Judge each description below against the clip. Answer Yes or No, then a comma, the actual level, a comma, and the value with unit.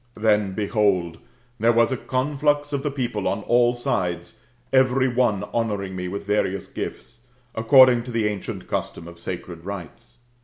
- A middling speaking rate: Yes, average, 155 wpm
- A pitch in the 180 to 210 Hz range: No, low, 110 Hz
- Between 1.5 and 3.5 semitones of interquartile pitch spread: No, average, 4.4 semitones